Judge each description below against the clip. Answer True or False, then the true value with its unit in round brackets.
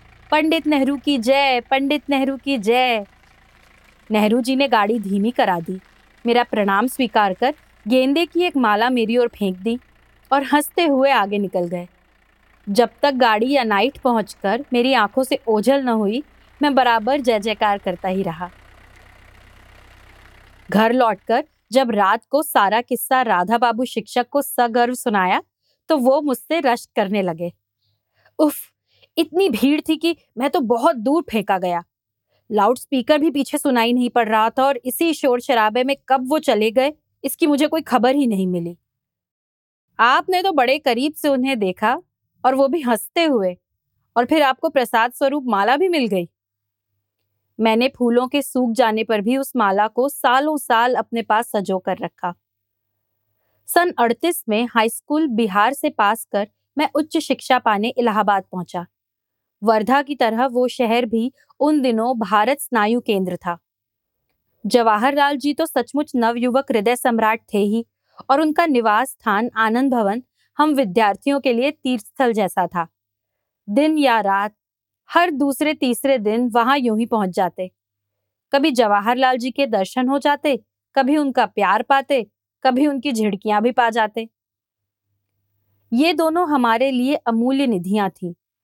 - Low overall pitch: False (240 Hz)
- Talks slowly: False (155 wpm)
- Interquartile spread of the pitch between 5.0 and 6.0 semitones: True (5.4 semitones)